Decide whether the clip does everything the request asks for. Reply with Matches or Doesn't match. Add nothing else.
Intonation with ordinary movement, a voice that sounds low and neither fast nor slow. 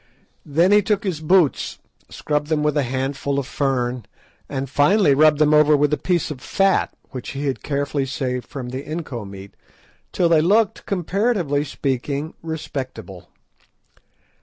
Doesn't match